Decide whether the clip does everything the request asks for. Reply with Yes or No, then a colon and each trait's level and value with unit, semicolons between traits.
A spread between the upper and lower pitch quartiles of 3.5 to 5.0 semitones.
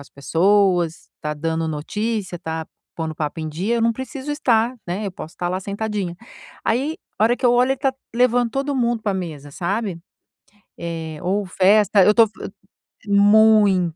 No: wide, 5.5 semitones